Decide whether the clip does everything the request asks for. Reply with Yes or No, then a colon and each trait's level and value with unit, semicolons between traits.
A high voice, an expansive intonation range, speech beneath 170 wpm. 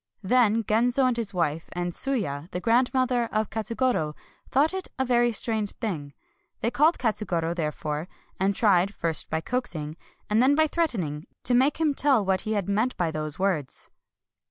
No: high, 215 Hz; wide, 6.6 semitones; average, 175 wpm